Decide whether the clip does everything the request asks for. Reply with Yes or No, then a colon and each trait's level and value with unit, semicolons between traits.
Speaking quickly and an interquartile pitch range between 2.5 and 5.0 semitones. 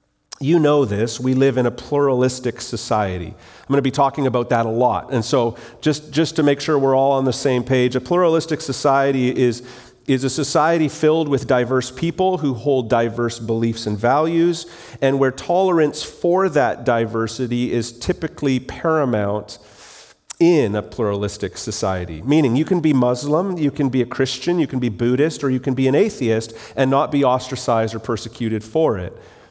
No: average, 180 wpm; average, 3.8 semitones